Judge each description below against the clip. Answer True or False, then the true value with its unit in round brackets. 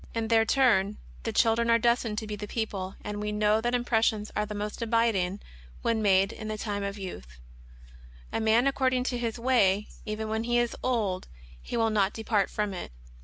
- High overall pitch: True (220 Hz)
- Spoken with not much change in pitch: True (2.1 semitones)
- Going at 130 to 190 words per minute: False (205 wpm)